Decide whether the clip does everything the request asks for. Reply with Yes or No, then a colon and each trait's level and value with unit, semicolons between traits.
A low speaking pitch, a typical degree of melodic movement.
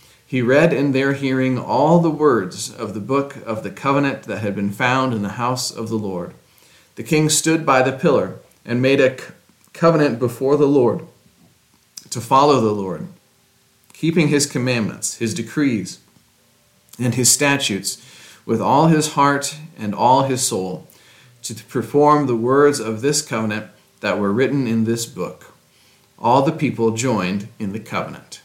Yes: low, 130 Hz; average, 3.9 semitones